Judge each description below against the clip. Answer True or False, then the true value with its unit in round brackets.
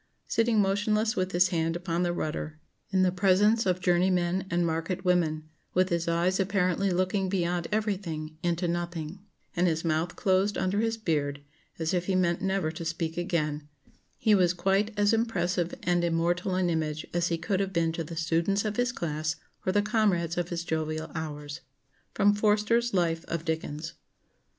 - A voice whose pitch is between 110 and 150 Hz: False (175 Hz)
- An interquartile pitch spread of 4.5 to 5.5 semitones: False (2.8 semitones)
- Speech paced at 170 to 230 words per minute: True (180 wpm)